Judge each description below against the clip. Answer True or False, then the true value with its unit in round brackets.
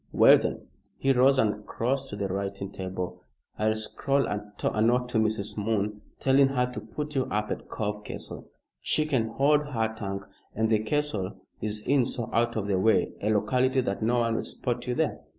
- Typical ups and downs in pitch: True (3.8 semitones)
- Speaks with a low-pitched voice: True (110 Hz)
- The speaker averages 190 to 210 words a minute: True (195 wpm)